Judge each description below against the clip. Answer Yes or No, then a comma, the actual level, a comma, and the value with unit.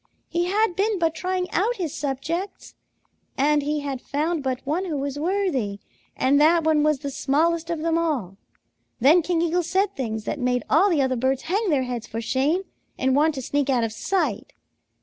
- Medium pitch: No, very high, 300 Hz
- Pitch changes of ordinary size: Yes, average, 4.6 semitones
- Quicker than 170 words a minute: Yes, average, 195 wpm